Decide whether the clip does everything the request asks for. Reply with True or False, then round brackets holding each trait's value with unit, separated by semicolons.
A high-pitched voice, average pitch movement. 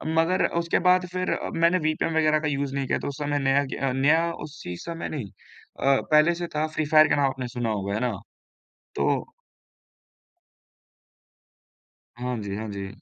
False (145 Hz; 4.0 semitones)